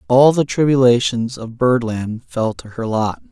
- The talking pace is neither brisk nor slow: Yes, average, 165 wpm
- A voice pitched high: No, low, 120 Hz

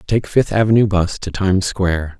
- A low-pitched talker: Yes, very low, 95 Hz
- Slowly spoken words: No, average, 190 wpm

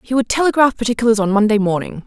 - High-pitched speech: Yes, high, 225 Hz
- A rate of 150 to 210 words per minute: Yes, fast, 205 wpm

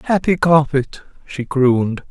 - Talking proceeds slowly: Yes, slow, 115 wpm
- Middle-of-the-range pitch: Yes, medium, 145 Hz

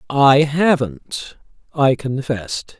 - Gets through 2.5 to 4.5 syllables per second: Yes, 3.1 syllables/s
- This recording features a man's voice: Yes, male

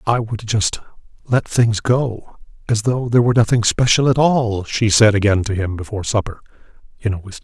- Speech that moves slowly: No, average, 195 wpm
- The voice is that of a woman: No, male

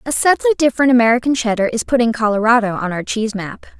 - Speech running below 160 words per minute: No, average, 190 wpm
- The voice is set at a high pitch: Yes, high, 235 Hz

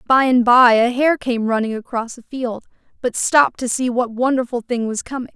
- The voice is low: No, high, 245 Hz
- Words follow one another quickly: Yes, fast, 215 wpm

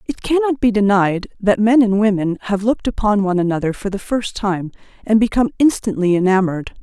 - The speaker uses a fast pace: No, average, 185 wpm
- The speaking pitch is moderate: No, high, 205 Hz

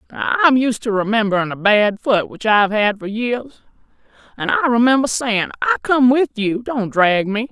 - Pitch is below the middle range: No, high, 230 Hz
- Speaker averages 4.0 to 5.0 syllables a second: Yes, 4.8 syllables/s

